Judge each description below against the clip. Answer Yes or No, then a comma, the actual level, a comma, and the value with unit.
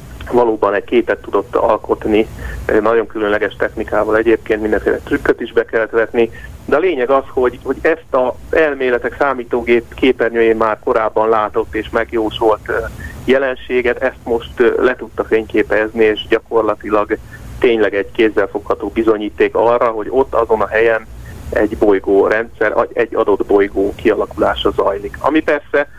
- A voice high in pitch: No, low, 120 Hz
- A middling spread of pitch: No, wide, 7.2 semitones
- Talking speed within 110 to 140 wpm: Yes, average, 135 wpm